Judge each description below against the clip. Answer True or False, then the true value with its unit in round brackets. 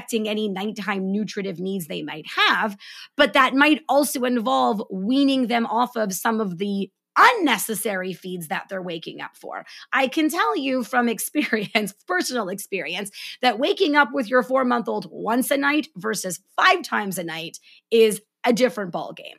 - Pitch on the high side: True (225 Hz)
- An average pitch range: True (4.8 semitones)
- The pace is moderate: True (170 wpm)